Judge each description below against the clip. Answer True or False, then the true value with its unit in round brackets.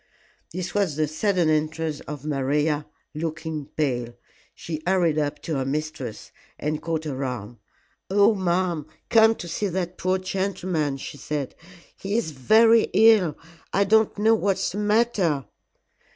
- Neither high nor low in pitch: True (160 Hz)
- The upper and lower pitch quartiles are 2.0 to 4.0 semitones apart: False (4.7 semitones)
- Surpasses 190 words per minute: False (145 wpm)